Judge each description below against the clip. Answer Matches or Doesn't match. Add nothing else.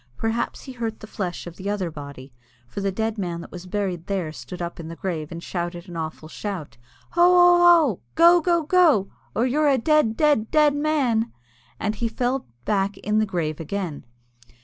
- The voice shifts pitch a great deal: Matches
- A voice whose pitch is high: Matches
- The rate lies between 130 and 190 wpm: Doesn't match